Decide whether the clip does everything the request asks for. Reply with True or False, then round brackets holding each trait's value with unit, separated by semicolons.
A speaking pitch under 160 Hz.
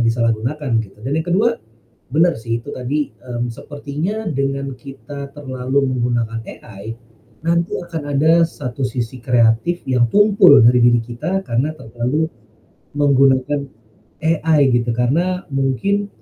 True (135 Hz)